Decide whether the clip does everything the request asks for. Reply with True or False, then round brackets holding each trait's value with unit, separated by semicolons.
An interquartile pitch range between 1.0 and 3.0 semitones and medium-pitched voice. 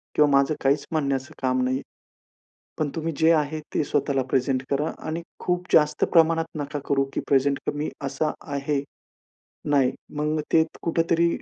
True (2.4 semitones; 145 Hz)